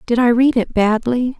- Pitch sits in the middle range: No, high, 240 Hz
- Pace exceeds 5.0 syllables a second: No, 4.7 syllables/s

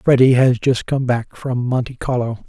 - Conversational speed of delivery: Yes, average, 195 wpm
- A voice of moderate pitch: No, low, 125 Hz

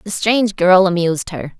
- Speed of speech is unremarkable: Yes, average, 190 wpm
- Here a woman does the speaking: Yes, female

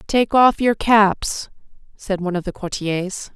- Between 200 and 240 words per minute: No, average, 160 wpm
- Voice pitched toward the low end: No, high, 200 Hz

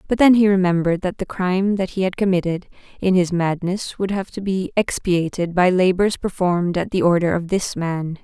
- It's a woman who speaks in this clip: Yes, female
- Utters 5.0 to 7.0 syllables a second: Yes, 5.3 syllables/s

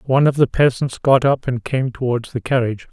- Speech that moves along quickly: Yes, fast, 225 wpm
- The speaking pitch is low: Yes, low, 125 Hz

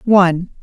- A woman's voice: Yes, female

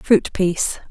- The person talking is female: Yes, female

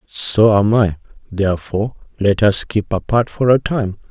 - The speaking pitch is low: Yes, low, 105 Hz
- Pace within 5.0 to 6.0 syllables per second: No, 4.5 syllables/s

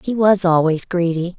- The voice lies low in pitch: No, medium, 180 Hz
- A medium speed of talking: Yes, average, 175 wpm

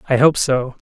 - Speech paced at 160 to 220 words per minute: Yes, fast, 205 wpm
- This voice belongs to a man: Yes, male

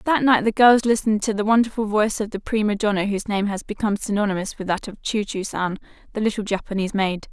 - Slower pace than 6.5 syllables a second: No, 6.6 syllables/s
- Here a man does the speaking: No, female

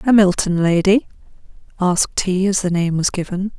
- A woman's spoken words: Yes, female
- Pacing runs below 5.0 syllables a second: No, 5.1 syllables/s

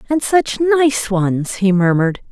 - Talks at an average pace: Yes, average, 155 wpm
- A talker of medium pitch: No, high, 225 Hz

